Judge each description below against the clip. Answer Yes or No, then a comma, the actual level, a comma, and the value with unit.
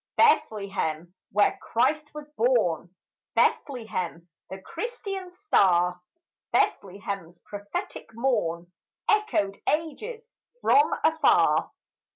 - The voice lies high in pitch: Yes, high, 210 Hz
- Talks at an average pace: No, slow, 80 wpm